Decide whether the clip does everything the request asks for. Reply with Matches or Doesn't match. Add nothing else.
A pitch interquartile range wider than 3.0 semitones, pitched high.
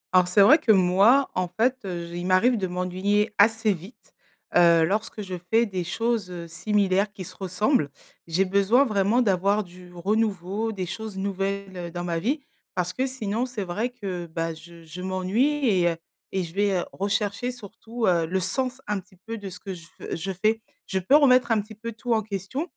Matches